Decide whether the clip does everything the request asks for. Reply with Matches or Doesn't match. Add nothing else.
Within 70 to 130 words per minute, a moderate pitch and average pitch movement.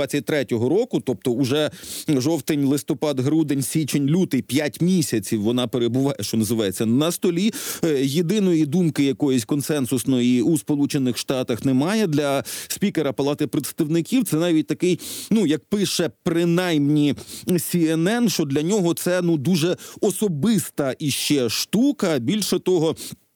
Matches